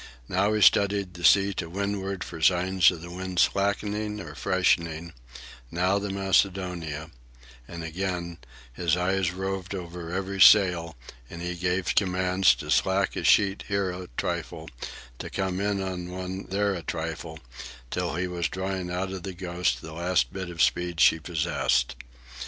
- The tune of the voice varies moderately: No, narrow, 2.0 semitones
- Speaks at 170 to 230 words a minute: No, average, 160 wpm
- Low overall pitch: Yes, very low, 90 Hz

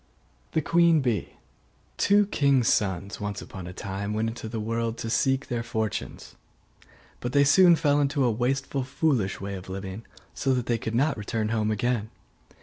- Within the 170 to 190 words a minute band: Yes, average, 175 wpm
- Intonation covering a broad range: No, average, 4.6 semitones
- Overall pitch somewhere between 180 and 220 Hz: No, low, 115 Hz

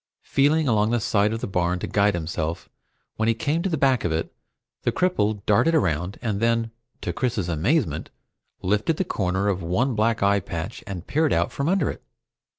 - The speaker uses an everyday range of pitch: No, wide, 6.4 semitones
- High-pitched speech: No, low, 105 Hz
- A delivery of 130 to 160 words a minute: No, average, 195 wpm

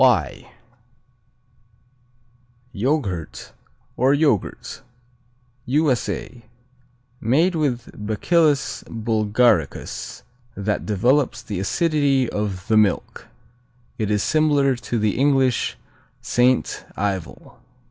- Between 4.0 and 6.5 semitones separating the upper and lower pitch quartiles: Yes, average, 5.2 semitones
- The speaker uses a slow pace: Yes, slow, 80 wpm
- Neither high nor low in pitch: No, low, 120 Hz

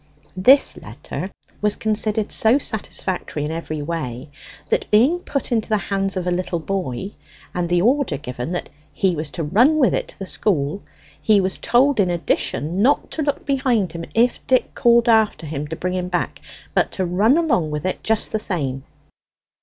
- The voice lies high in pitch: Yes, high, 195 Hz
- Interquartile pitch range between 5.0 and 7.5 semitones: Yes, wide, 5.4 semitones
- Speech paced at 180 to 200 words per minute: Yes, average, 185 wpm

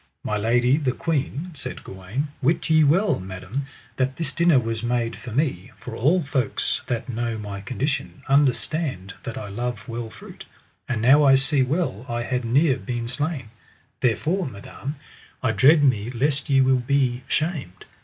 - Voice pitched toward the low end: Yes, low, 130 Hz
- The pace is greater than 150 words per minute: Yes, average, 165 wpm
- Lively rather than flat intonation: No, average, 3.7 semitones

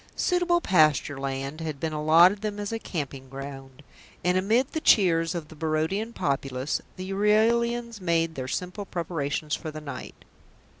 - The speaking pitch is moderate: Yes, medium, 165 Hz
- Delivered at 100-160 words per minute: Yes, average, 155 wpm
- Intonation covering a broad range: Yes, wide, 6.0 semitones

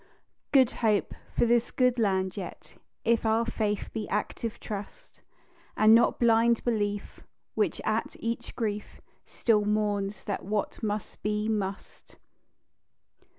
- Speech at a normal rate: No, slow, 125 wpm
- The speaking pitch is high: Yes, high, 215 Hz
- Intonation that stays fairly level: Yes, narrow, 2.1 semitones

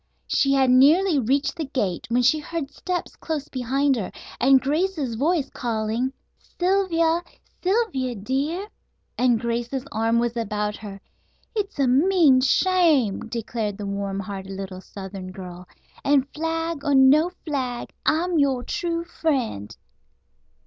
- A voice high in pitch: Yes, very high, 265 Hz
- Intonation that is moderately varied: No, wide, 6.3 semitones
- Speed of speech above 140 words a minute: No, slow, 135 wpm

